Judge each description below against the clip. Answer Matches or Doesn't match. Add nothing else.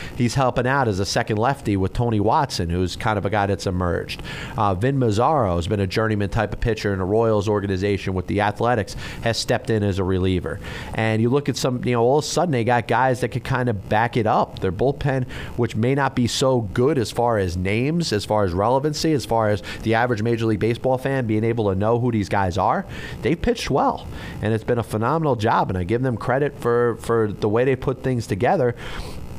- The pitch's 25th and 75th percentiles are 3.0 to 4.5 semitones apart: Matches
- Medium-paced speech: Doesn't match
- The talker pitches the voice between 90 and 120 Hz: Matches